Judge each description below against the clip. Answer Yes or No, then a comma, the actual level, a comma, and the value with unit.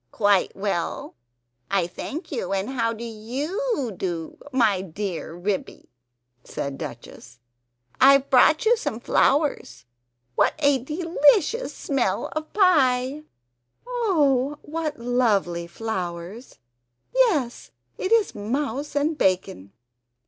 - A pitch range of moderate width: No, wide, 7.6 semitones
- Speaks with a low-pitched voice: No, very high, 250 Hz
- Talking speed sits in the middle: No, slow, 105 wpm